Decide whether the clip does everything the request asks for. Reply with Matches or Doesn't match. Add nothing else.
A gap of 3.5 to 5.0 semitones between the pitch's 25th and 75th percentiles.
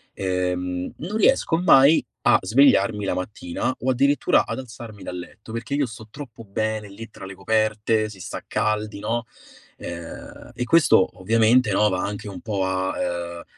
Matches